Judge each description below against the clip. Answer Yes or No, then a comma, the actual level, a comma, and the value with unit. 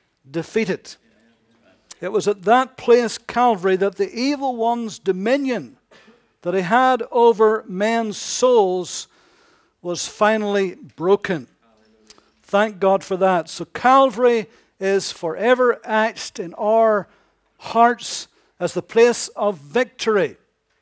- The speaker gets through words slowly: Yes, slow, 110 wpm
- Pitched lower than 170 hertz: No, high, 215 Hz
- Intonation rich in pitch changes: No, average, 4.3 semitones